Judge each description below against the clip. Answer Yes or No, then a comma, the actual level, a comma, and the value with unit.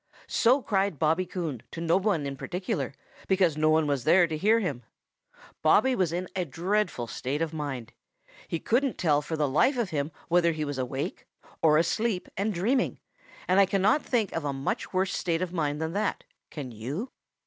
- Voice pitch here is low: No, medium, 170 Hz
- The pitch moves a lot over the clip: No, average, 4.8 semitones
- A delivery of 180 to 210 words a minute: Yes, average, 190 wpm